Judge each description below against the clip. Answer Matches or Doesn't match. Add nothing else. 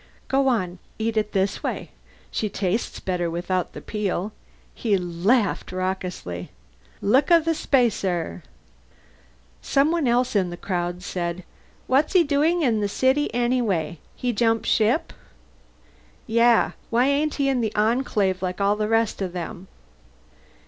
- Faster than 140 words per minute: Doesn't match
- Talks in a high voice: Matches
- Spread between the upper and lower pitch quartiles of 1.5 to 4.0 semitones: Doesn't match